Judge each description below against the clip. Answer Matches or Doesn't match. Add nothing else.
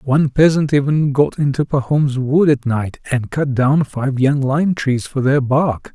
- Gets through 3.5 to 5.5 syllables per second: Matches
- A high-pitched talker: Doesn't match